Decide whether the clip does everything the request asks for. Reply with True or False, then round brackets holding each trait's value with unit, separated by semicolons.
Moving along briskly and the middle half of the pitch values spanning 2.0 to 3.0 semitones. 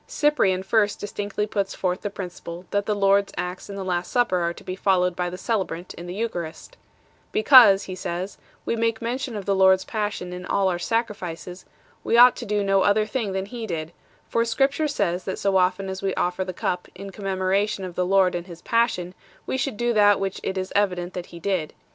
True (230 wpm; 2.7 semitones)